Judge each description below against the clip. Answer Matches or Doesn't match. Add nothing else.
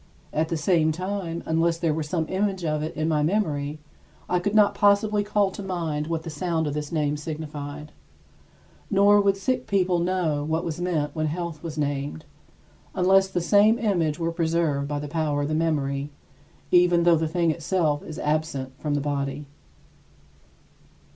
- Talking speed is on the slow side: Doesn't match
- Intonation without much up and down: Doesn't match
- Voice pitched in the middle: Matches